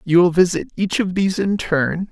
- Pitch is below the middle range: No, medium, 180 Hz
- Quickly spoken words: Yes, fast, 225 wpm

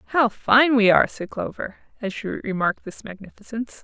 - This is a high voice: Yes, high, 220 Hz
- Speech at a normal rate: Yes, average, 170 wpm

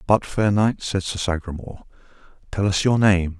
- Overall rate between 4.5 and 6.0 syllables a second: Yes, 5.1 syllables/s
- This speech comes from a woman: No, male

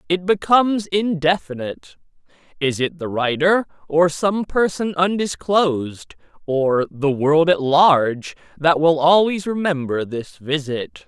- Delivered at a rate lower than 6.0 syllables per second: Yes, 4.0 syllables/s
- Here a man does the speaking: Yes, male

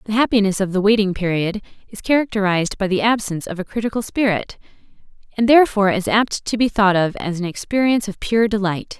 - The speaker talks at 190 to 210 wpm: Yes, average, 195 wpm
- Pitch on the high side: Yes, high, 205 Hz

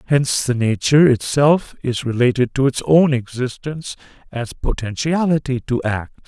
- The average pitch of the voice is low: Yes, low, 130 Hz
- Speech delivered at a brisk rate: No, slow, 135 wpm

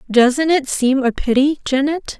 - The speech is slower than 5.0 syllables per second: Yes, 4.1 syllables/s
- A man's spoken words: No, female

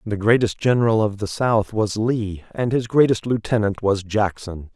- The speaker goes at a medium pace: Yes, average, 175 wpm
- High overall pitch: No, low, 110 Hz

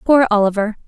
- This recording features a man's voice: No, female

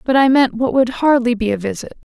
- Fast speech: Yes, fast, 255 wpm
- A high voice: Yes, high, 245 Hz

